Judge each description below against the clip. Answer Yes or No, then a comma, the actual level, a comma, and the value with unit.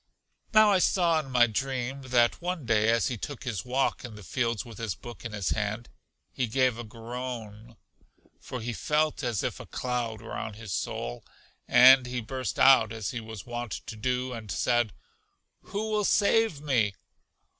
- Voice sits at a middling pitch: No, low, 120 Hz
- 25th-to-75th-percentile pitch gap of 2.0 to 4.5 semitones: Yes, average, 2.9 semitones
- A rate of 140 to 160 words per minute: No, average, 185 wpm